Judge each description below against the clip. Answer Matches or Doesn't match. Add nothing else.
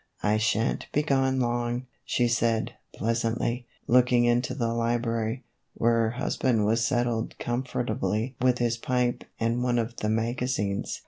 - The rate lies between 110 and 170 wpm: Matches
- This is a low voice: Matches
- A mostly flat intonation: Matches